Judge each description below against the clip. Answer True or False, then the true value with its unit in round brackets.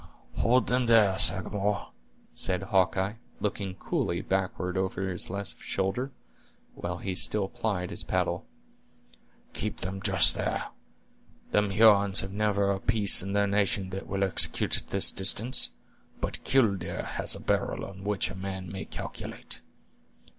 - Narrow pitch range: True (1.6 semitones)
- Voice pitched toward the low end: True (100 Hz)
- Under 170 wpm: True (145 wpm)